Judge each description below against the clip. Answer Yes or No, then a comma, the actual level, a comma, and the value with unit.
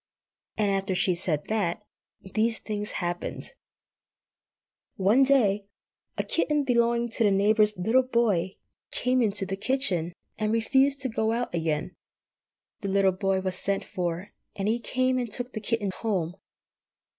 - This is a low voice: No, high, 210 Hz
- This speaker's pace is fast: No, average, 150 wpm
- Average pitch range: Yes, average, 3.9 semitones